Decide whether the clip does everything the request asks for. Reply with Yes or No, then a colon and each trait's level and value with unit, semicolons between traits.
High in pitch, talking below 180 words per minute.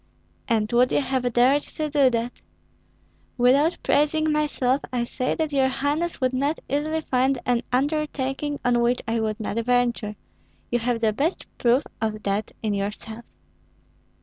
Yes: very high, 255 Hz; average, 155 wpm